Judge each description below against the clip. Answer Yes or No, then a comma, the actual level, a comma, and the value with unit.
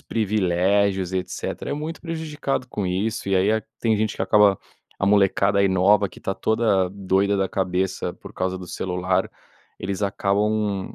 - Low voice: Yes, low, 100 Hz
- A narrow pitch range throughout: Yes, narrow, 2.2 semitones